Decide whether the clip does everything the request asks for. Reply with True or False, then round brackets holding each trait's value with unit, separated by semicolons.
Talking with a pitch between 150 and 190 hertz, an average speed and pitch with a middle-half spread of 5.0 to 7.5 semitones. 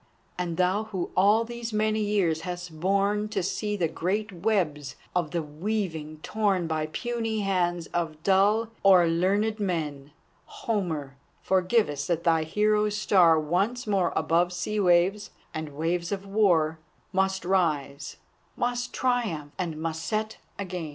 False (185 Hz; 145 wpm; 4.4 semitones)